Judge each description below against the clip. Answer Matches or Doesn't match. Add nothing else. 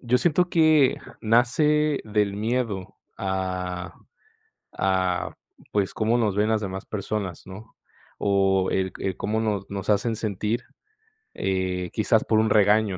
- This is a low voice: Matches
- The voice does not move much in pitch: Doesn't match